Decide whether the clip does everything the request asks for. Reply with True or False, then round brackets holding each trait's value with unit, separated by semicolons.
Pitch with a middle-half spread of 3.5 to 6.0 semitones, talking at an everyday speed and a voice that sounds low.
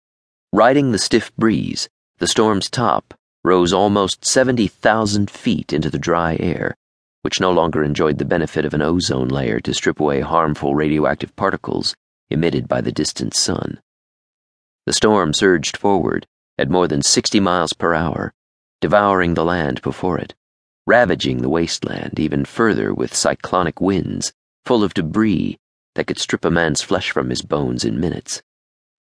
True (5.1 semitones; 150 wpm; 75 Hz)